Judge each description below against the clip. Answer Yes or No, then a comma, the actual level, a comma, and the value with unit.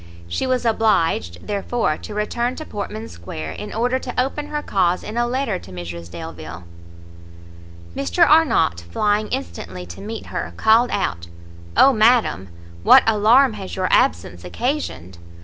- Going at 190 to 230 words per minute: No, average, 150 wpm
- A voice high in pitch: Yes, high, 205 Hz